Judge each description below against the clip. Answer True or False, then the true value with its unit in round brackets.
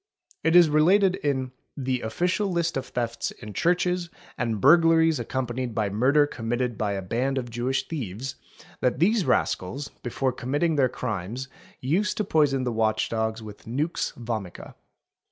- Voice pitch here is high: False (130 Hz)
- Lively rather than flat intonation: True (5.9 semitones)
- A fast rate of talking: False (155 wpm)